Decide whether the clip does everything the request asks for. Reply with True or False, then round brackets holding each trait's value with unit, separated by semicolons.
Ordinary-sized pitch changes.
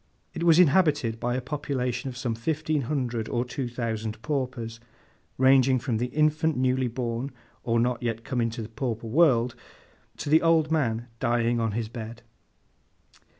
True (3.5 semitones)